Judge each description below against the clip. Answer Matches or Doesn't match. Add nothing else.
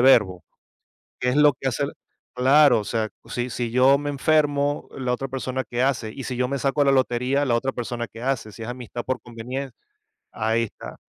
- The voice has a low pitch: Matches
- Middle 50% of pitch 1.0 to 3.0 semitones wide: Matches